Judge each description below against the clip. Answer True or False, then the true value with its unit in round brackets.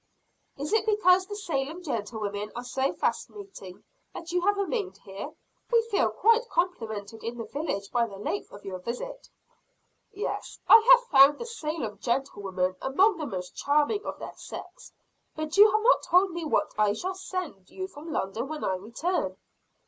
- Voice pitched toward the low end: False (300 Hz)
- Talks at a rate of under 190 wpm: True (170 wpm)